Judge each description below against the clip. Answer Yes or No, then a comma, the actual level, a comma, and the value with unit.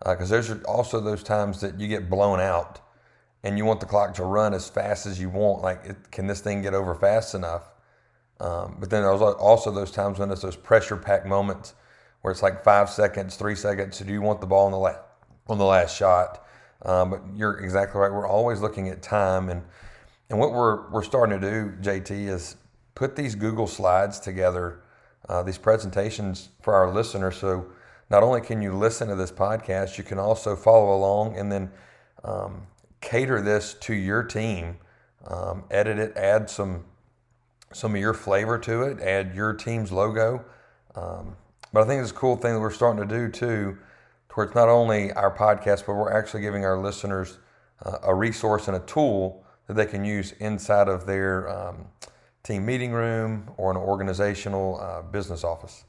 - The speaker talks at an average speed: Yes, average, 195 wpm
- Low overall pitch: Yes, low, 100 Hz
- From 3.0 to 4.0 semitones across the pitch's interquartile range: No, narrow, 2.5 semitones